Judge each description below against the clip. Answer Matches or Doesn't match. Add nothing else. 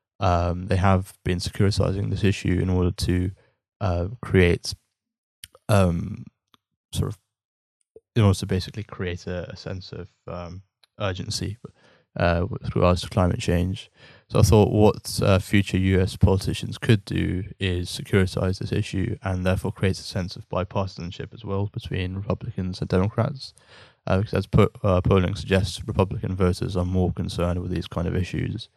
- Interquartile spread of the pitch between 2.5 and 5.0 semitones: Matches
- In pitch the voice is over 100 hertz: Doesn't match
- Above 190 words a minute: Doesn't match